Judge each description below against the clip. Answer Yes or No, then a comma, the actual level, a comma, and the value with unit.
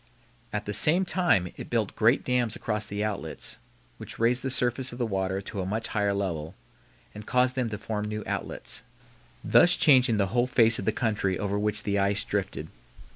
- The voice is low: Yes, low, 105 Hz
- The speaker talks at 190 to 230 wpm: Yes, average, 195 wpm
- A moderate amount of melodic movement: Yes, average, 3.3 semitones